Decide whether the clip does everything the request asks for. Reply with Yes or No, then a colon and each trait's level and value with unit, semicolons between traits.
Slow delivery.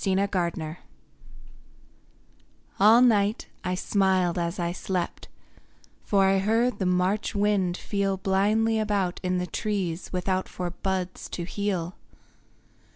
Yes: slow, 115 wpm